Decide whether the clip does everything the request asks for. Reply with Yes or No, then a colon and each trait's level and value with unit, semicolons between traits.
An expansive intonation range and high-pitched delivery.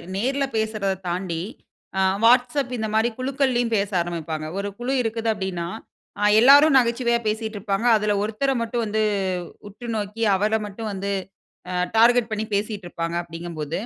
No: average, 3.5 semitones; high, 220 Hz